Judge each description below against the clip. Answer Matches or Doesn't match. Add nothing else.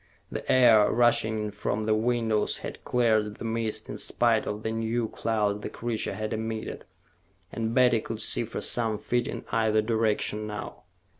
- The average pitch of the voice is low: Matches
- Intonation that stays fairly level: Matches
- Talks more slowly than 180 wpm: Matches